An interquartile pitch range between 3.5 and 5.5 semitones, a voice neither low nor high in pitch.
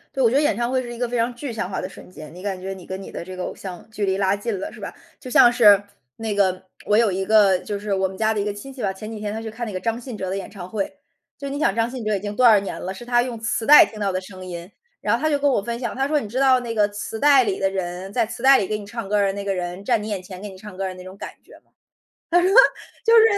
No: average, 3.9 semitones; high, 210 Hz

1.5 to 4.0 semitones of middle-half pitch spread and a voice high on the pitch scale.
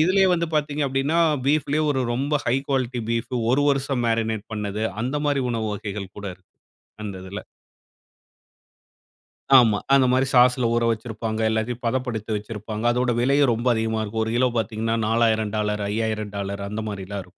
No: average, 3.6 semitones; low, 115 Hz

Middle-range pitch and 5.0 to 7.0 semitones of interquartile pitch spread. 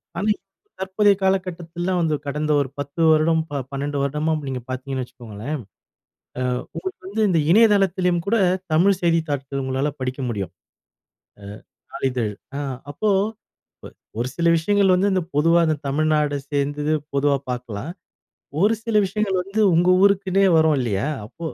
Yes: medium, 160 Hz; average, 5.3 semitones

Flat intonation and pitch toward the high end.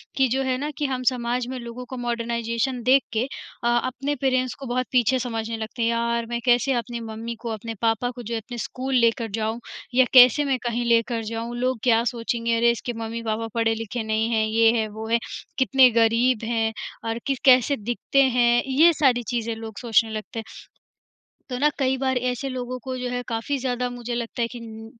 Yes: narrow, 1.9 semitones; high, 235 Hz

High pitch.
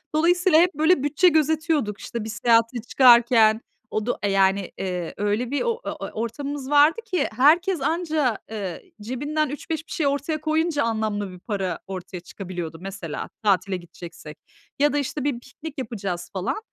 Yes: high, 245 Hz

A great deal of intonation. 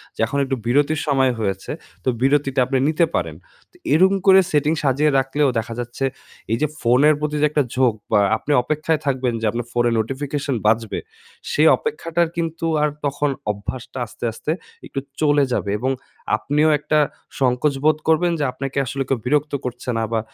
No: average, 3.3 semitones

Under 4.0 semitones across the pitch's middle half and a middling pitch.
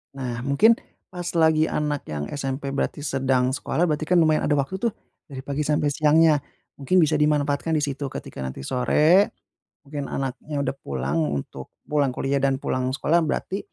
Yes: average, 2.7 semitones; medium, 145 Hz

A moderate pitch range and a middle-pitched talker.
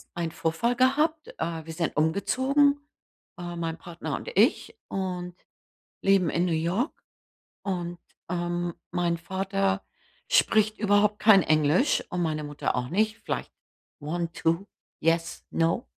Yes: average, 4.0 semitones; medium, 175 Hz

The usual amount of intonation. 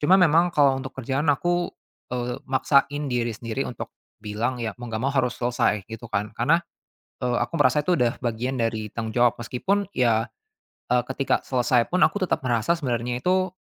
Yes: average, 3.6 semitones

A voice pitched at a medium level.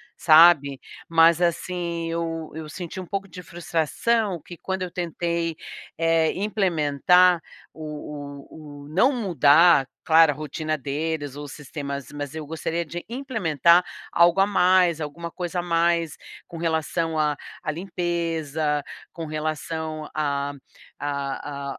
Yes: medium, 165 Hz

